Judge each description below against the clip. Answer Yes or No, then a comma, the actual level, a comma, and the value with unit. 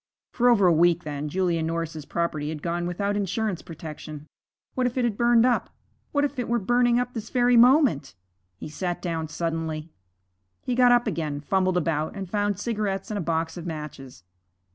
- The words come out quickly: No, average, 190 wpm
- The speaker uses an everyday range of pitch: No, wide, 6.6 semitones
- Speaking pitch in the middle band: Yes, medium, 180 Hz